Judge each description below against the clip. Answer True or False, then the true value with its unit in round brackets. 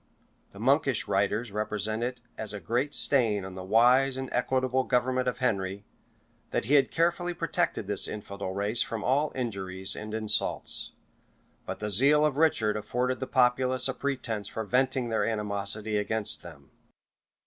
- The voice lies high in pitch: False (115 Hz)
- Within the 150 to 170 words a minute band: True (160 wpm)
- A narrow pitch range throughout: False (4.0 semitones)